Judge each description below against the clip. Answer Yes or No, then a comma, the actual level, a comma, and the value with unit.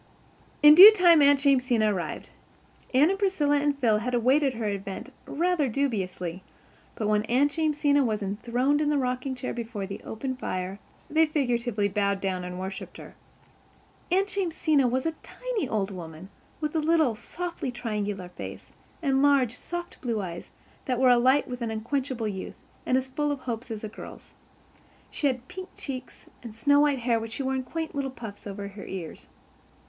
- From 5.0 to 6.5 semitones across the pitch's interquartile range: Yes, average, 5.3 semitones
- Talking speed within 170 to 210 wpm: Yes, average, 175 wpm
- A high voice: Yes, very high, 255 Hz